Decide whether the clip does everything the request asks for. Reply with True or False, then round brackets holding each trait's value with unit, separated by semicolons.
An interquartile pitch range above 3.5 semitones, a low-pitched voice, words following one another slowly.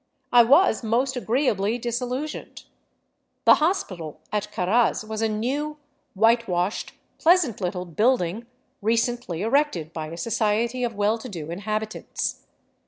False (3.9 semitones; 225 Hz; 125 wpm)